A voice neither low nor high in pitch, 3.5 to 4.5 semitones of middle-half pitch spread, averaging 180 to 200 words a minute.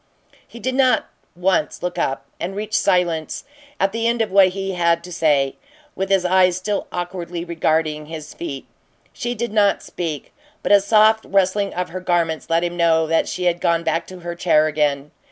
No: medium, 175 Hz; average, 3.0 semitones; average, 190 wpm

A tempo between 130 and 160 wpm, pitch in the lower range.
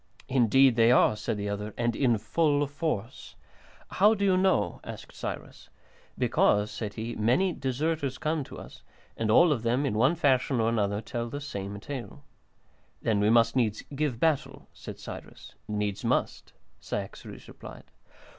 Yes: average, 155 wpm; low, 120 Hz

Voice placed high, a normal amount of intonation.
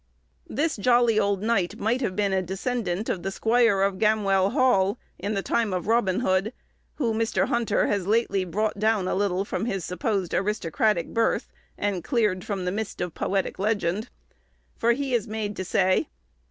Yes: high, 205 Hz; average, 3.2 semitones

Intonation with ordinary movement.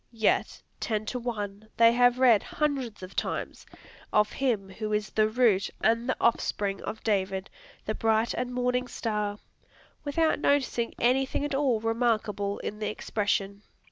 Yes: average, 3.0 semitones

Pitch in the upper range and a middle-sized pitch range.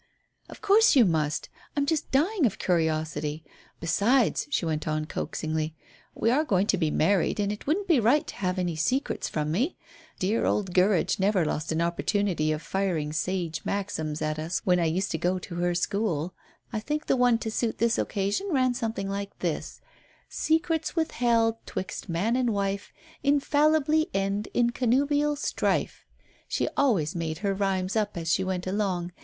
No: high, 195 Hz; wide, 6.5 semitones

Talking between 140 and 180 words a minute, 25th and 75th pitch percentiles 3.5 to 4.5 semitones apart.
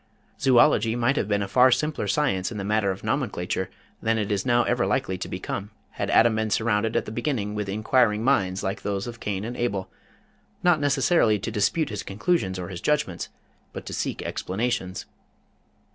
No: average, 190 wpm; average, 3.8 semitones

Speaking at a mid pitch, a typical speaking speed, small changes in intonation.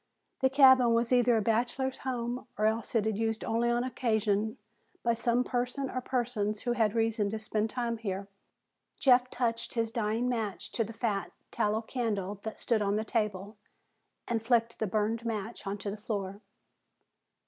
No: high, 225 Hz; average, 170 wpm; narrow, 2.2 semitones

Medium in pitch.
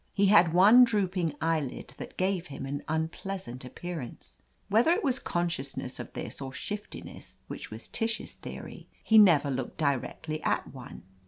Yes: medium, 170 Hz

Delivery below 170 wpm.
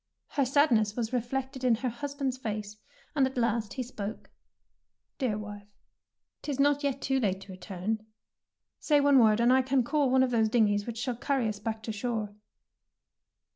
No: average, 175 wpm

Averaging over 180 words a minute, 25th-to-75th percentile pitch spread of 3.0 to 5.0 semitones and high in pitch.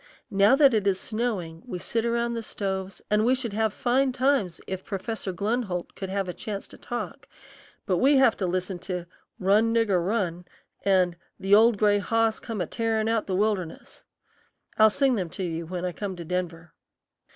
Yes: average, 190 wpm; average, 3.8 semitones; high, 200 Hz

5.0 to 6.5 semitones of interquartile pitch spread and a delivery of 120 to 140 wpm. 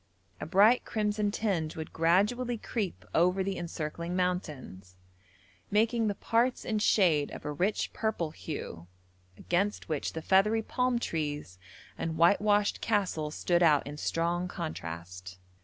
Yes: average, 5.3 semitones; slow, 135 wpm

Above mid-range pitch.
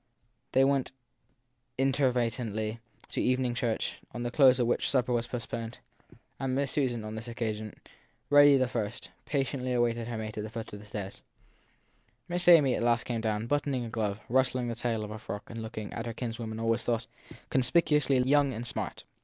No: low, 120 Hz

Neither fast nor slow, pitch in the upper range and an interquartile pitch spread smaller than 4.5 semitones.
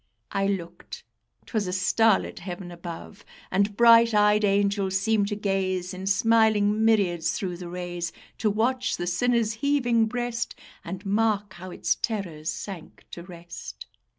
Yes: average, 145 wpm; high, 200 Hz; average, 3.5 semitones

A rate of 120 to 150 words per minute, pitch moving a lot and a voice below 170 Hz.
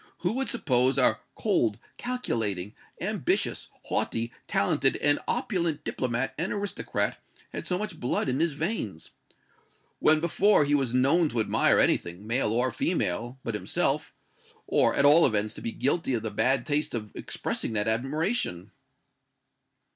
Yes: average, 145 wpm; wide, 6.4 semitones; low, 135 Hz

